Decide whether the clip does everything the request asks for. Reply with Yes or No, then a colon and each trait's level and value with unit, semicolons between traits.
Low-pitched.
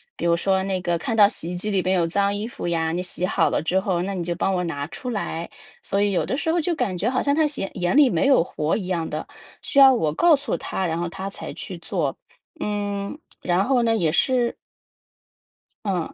No: high, 190 Hz